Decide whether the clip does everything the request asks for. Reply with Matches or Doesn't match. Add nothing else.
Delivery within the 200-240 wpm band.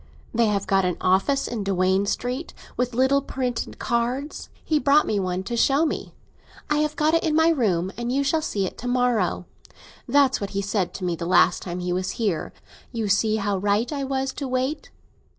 Matches